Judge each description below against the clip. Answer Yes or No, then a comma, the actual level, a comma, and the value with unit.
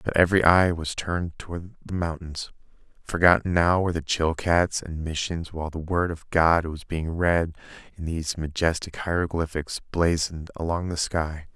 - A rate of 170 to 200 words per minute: No, average, 160 wpm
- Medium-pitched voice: No, very low, 85 Hz